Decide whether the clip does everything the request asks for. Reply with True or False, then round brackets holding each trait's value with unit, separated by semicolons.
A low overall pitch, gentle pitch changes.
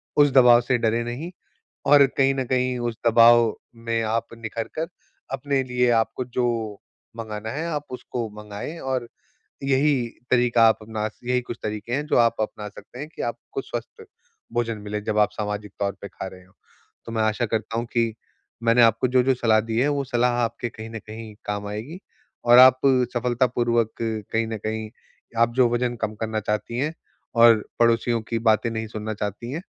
True (115 Hz; 2.3 semitones)